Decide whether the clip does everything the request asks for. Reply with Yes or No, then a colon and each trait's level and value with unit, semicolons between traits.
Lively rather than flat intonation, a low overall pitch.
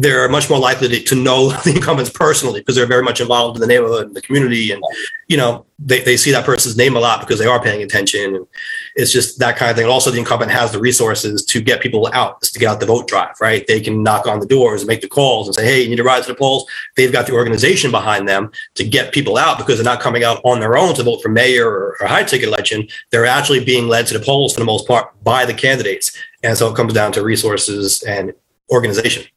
Yes: wide, 6.8 semitones; low, 125 Hz